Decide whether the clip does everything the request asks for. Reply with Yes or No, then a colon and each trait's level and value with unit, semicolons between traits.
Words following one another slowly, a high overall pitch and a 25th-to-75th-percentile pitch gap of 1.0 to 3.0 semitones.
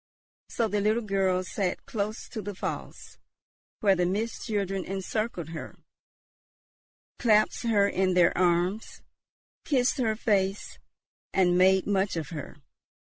Yes: slow, 130 wpm; high, 195 Hz; average, 2.7 semitones